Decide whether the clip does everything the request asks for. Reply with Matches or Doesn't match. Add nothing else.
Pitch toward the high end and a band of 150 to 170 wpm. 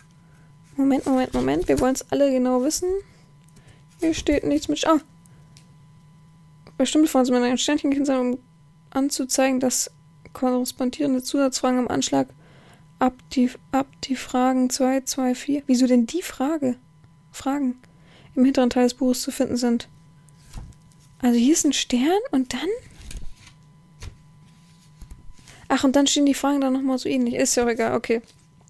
Matches